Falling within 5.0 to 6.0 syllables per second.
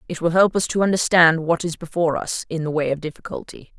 No: 6.3 syllables/s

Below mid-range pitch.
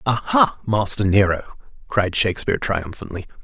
Yes: low, 105 Hz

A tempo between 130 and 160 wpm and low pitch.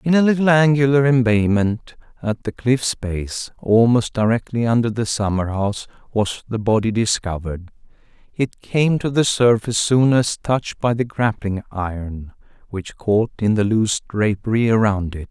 Yes: average, 155 wpm; low, 115 Hz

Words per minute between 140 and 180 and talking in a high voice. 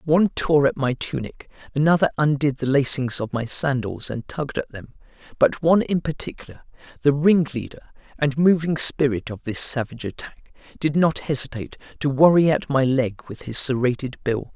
No: average, 170 wpm; medium, 140 Hz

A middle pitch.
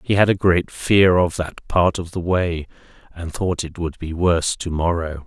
No: very low, 85 Hz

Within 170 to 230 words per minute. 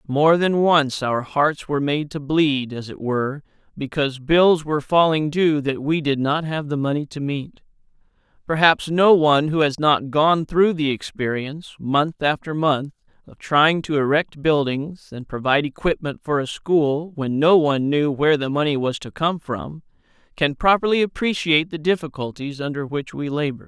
Yes: average, 175 wpm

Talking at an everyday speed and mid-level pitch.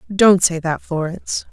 Yes: average, 160 wpm; medium, 175 Hz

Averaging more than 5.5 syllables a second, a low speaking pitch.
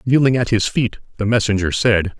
No: 5.4 syllables/s; low, 110 Hz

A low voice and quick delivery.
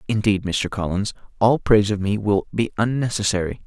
No: low, 105 Hz; average, 165 wpm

